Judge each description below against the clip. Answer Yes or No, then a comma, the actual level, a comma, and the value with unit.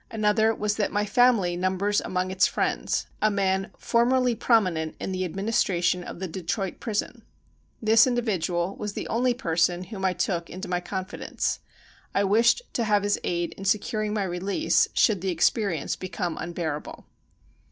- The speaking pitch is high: Yes, high, 195 Hz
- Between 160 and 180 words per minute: Yes, average, 175 wpm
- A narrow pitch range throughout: No, average, 3.3 semitones